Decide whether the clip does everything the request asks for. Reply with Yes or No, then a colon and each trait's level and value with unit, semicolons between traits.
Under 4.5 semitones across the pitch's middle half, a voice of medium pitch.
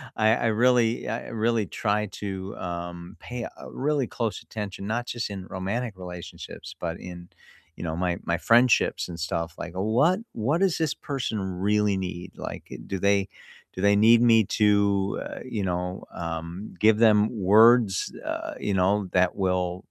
No: average, 3.8 semitones; low, 100 Hz